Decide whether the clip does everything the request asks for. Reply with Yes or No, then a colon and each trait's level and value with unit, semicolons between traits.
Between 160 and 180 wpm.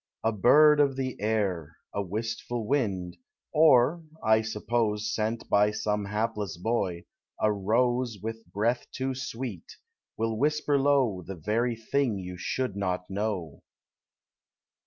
No: slow, 135 wpm